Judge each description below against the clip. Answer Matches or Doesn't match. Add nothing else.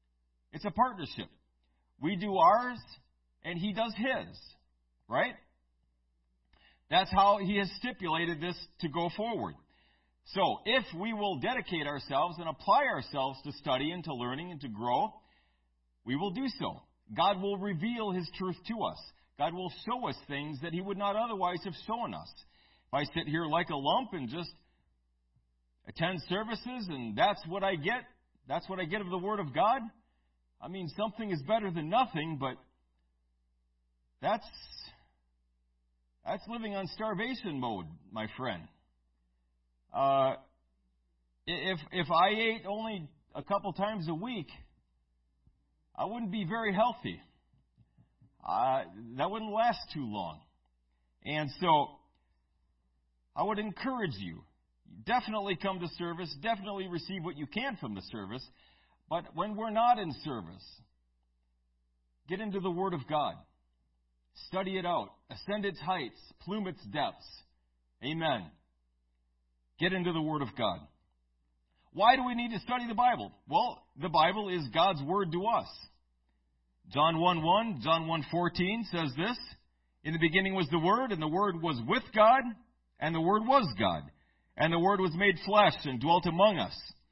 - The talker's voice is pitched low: Doesn't match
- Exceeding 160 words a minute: Doesn't match